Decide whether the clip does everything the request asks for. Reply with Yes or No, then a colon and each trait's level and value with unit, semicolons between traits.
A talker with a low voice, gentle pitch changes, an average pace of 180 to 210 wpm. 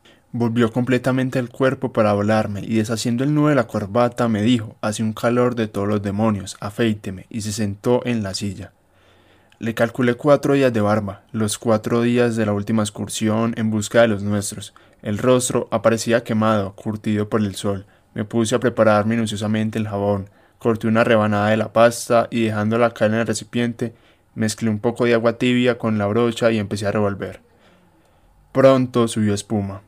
Yes: low, 110 Hz; narrow, 2.3 semitones; average, 185 wpm